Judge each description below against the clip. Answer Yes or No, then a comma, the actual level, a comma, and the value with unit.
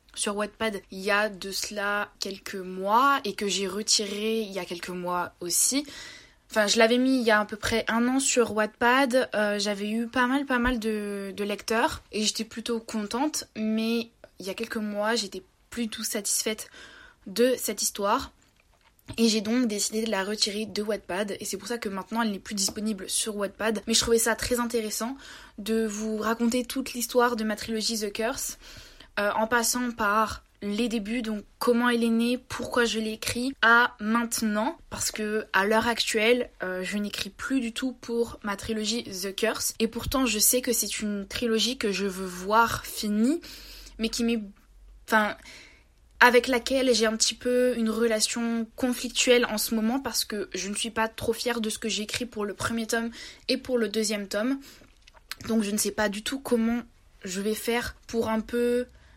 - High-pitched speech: Yes, high, 225 Hz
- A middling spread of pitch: No, narrow, 2.3 semitones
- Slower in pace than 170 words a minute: No, average, 195 wpm